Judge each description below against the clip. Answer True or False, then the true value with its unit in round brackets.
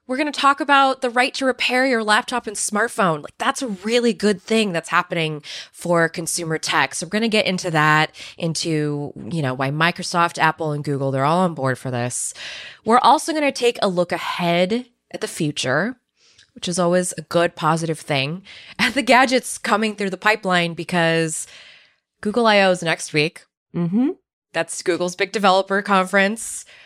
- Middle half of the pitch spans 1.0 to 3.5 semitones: False (5.5 semitones)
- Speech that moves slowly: False (180 wpm)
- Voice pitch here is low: False (180 Hz)